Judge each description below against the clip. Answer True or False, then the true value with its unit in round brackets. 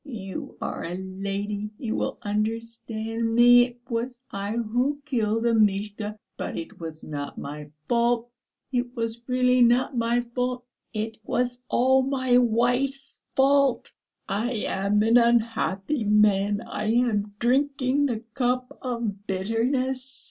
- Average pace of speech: False (130 wpm)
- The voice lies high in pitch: True (235 Hz)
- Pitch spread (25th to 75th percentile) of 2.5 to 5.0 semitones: True (3.0 semitones)